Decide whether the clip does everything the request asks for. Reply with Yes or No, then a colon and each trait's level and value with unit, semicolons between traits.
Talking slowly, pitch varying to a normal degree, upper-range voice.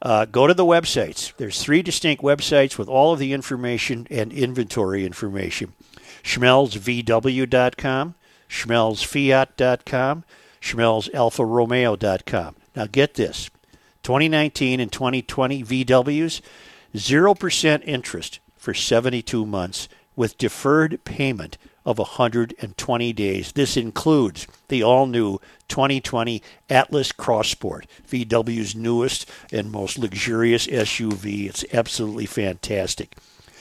No: slow, 100 wpm; average, 3.6 semitones; low, 125 Hz